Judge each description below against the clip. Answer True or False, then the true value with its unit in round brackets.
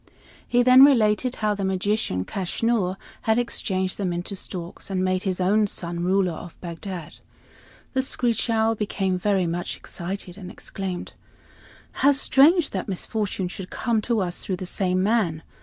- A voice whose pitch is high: True (195 Hz)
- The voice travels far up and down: False (3.5 semitones)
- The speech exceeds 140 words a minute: True (160 wpm)